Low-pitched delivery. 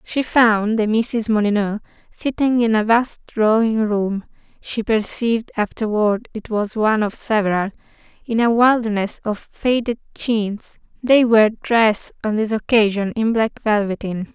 No: high, 220 Hz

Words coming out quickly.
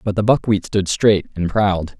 Yes: fast, 210 wpm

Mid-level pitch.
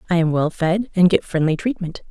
Yes: medium, 175 Hz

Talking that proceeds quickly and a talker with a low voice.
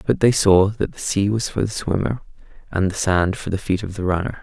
Yes: fast, 255 wpm; low, 100 Hz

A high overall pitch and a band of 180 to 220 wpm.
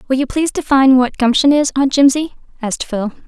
Yes: very high, 265 Hz; average, 200 wpm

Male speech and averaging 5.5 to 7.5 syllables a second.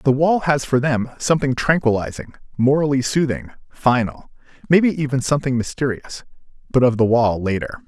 Yes: male; 5.6 syllables/s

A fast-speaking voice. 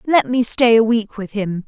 Yes: fast, 250 wpm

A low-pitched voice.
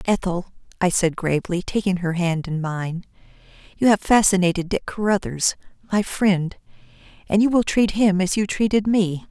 No: medium, 185 Hz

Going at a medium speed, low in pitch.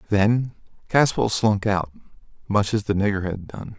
Yes: average, 160 wpm; low, 105 Hz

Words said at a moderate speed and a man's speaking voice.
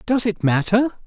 Yes: average, 170 wpm; male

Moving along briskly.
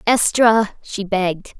No: slow, 115 wpm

